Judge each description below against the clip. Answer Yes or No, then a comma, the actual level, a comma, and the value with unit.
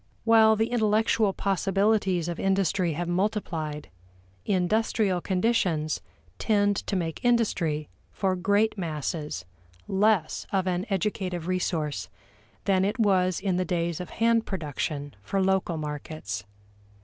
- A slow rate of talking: Yes, slow, 120 wpm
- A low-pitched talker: No, medium, 185 Hz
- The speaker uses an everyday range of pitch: Yes, average, 3.8 semitones